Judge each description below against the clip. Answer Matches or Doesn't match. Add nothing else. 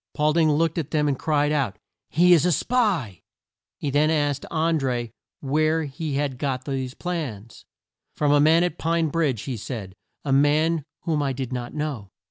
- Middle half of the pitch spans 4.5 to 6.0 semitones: Doesn't match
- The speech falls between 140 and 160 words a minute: Doesn't match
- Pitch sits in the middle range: Matches